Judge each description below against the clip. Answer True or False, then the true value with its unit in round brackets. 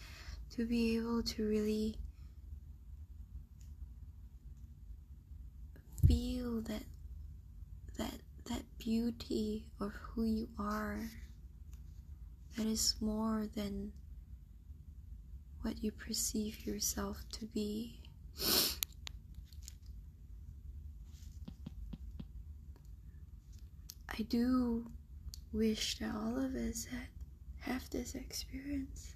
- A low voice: True (80 Hz)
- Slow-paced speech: True (70 wpm)